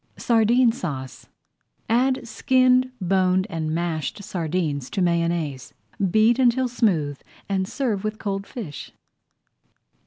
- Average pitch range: No, wide, 6.2 semitones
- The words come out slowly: Yes, slow, 105 wpm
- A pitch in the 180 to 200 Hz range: Yes, high, 190 Hz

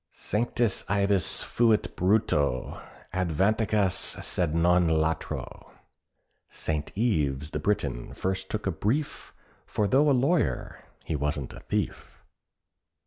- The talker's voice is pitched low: Yes, very low, 95 Hz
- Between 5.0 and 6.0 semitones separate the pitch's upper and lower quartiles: Yes, wide, 5.5 semitones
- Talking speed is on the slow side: Yes, slow, 110 wpm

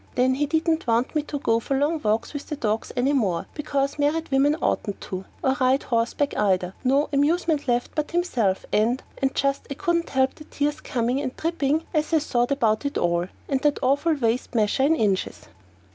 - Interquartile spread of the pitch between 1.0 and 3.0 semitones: No, average, 4.2 semitones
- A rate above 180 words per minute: Yes, average, 200 wpm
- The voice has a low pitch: No, very high, 275 Hz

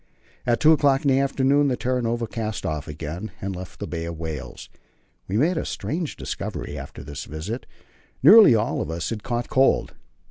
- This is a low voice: Yes, low, 115 Hz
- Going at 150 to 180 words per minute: No, average, 190 wpm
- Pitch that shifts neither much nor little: No, wide, 8.3 semitones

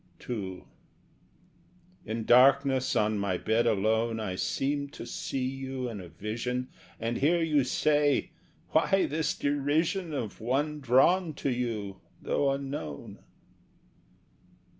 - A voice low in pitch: Yes, low, 130 Hz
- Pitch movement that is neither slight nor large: Yes, average, 4.5 semitones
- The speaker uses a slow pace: Yes, slow, 120 wpm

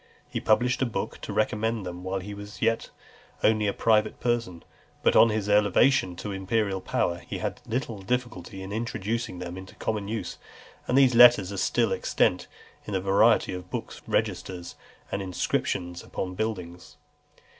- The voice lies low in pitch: Yes, low, 105 Hz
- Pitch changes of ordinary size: Yes, average, 3.3 semitones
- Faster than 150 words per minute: Yes, average, 165 wpm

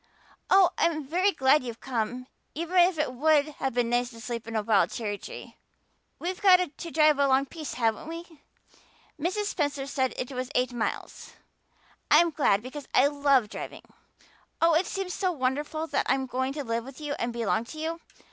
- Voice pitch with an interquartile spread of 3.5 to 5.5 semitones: Yes, average, 4.8 semitones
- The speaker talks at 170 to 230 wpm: Yes, average, 190 wpm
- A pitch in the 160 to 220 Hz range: No, very high, 280 Hz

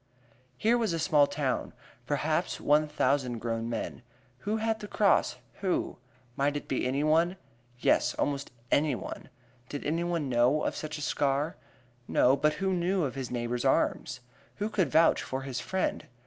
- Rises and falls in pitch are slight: No, average, 4.7 semitones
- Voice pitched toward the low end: No, medium, 145 Hz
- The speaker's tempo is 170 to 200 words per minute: No, average, 160 wpm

